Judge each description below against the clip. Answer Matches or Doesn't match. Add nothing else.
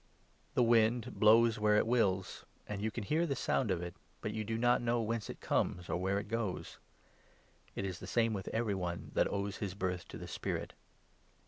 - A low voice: Matches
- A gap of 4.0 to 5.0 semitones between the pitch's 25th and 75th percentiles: Doesn't match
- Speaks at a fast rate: Matches